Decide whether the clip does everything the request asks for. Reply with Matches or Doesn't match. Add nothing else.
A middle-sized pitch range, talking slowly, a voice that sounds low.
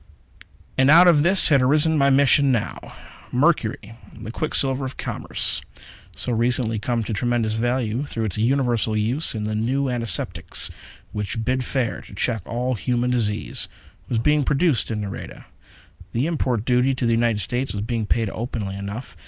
Doesn't match